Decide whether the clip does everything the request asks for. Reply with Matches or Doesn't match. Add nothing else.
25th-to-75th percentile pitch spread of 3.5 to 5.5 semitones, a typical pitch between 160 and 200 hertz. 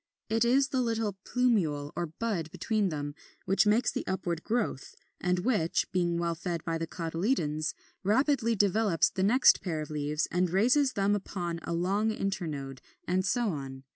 Matches